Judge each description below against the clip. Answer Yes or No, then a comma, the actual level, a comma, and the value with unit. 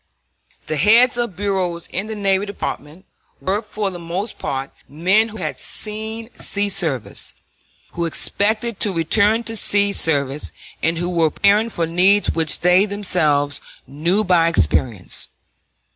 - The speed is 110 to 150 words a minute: Yes, average, 145 wpm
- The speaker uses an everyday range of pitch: Yes, average, 4.2 semitones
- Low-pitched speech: No, high, 190 Hz